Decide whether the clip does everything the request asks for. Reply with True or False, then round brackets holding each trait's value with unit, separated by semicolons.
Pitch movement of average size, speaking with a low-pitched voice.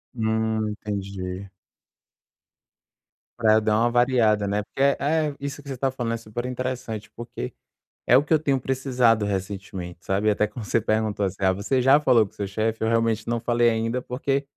True (3.3 semitones; 115 Hz)